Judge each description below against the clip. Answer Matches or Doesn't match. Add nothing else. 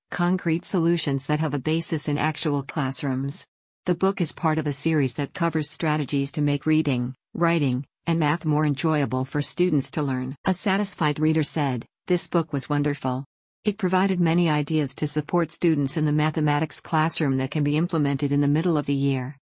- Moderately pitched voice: Matches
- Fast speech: Doesn't match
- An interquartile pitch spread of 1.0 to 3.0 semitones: Matches